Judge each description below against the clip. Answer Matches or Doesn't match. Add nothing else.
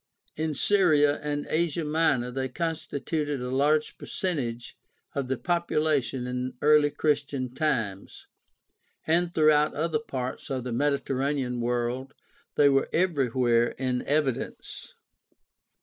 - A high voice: Doesn't match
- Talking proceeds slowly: Matches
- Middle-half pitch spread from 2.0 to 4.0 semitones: Matches